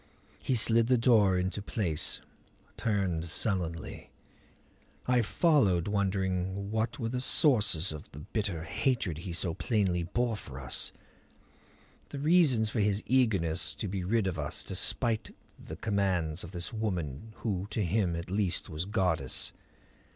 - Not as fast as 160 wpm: Yes, average, 145 wpm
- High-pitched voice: No, low, 100 Hz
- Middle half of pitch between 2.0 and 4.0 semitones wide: No, average, 4.5 semitones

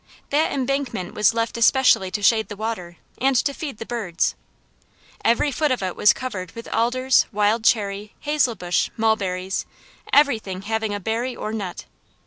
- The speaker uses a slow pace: No, average, 155 wpm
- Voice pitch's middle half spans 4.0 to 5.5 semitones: Yes, average, 4.3 semitones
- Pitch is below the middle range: No, high, 225 Hz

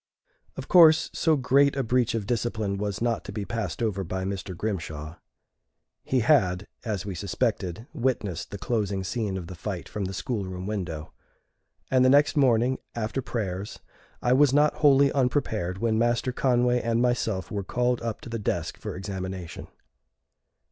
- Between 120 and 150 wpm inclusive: No, average, 170 wpm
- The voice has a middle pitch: No, low, 110 Hz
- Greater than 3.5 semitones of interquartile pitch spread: Yes, average, 4.7 semitones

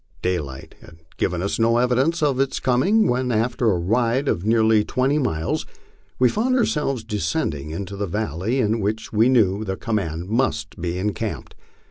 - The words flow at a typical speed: Yes, average, 170 wpm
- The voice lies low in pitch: Yes, low, 110 Hz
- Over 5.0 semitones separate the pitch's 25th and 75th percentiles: Yes, wide, 5.6 semitones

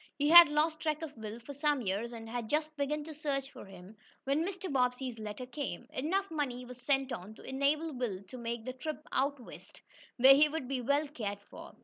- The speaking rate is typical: No, fast, 220 wpm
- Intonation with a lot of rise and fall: No, average, 4.0 semitones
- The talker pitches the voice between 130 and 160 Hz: No, very high, 270 Hz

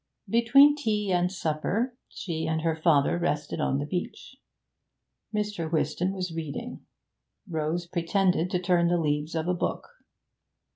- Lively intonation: No, average, 3.6 semitones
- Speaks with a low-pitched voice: No, medium, 175 Hz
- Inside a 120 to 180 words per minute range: Yes, average, 140 wpm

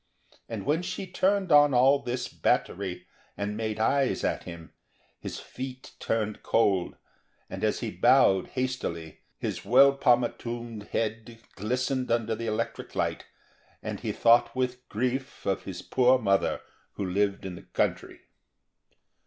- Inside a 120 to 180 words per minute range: Yes, average, 140 wpm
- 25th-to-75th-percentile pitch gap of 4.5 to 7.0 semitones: No, average, 3.9 semitones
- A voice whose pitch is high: No, low, 120 Hz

